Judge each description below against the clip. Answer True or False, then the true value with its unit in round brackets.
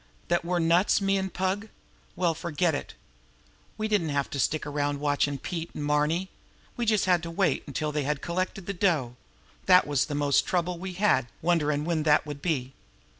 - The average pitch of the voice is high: False (165 Hz)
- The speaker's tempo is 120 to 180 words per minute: False (190 wpm)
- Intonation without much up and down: False (3.9 semitones)